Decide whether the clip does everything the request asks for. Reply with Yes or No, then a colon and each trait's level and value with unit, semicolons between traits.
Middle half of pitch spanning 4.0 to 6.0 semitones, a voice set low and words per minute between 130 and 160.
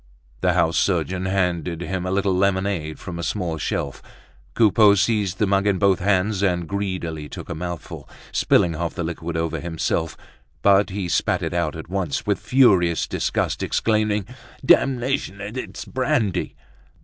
No: average, 3.1 semitones; very low, 95 Hz; average, 155 wpm